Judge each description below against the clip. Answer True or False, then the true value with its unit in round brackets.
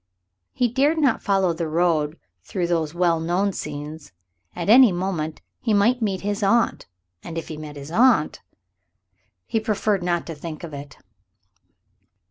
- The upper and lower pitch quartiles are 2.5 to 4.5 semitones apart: False (4.9 semitones)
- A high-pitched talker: False (175 Hz)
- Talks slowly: False (155 wpm)